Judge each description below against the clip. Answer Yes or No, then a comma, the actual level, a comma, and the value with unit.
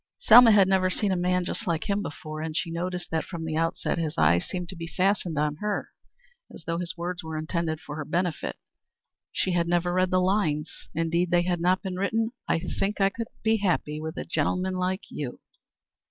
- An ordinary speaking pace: No, fast, 215 wpm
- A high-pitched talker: No, medium, 175 Hz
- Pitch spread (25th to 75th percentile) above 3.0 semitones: No, average, 2.7 semitones